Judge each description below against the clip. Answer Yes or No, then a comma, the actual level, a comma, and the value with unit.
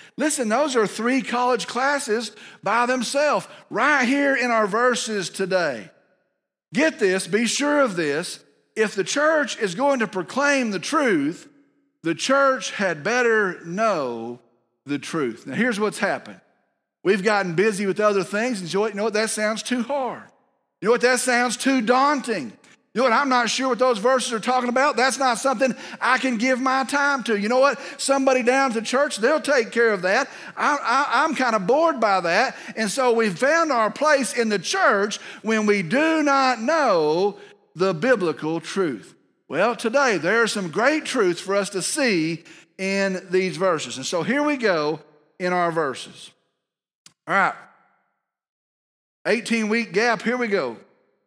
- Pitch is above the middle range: Yes, high, 235 Hz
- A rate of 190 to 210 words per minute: No, average, 175 wpm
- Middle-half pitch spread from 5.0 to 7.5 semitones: Yes, average, 5.3 semitones